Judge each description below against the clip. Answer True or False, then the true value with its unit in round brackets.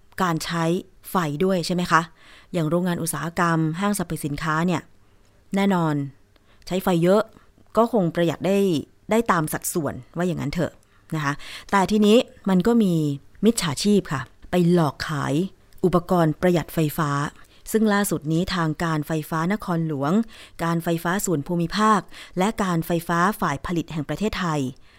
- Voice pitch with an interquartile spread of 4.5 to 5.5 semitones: False (3.5 semitones)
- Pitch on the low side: False (170 Hz)